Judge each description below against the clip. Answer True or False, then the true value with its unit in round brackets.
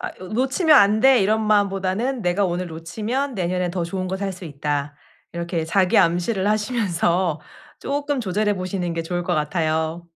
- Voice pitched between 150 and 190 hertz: True (185 Hz)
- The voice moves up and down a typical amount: True (3.9 semitones)